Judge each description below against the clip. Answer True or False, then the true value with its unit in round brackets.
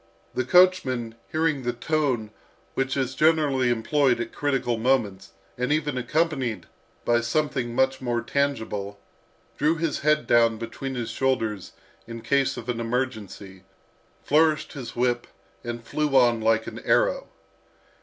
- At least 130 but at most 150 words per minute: True (135 wpm)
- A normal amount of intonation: True (3.8 semitones)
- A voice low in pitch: True (125 Hz)